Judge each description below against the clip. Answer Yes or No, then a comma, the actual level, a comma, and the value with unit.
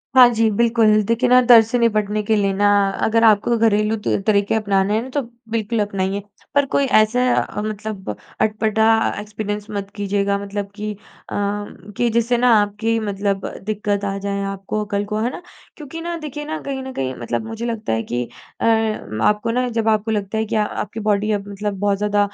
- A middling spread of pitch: No, narrow, 2.1 semitones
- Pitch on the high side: Yes, high, 215 Hz